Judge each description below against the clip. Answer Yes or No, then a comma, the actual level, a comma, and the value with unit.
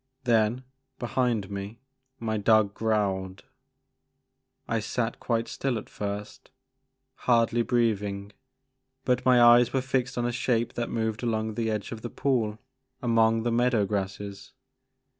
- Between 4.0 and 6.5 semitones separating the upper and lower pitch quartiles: No, narrow, 2.5 semitones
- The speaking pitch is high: No, low, 115 Hz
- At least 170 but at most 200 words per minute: No, slow, 135 wpm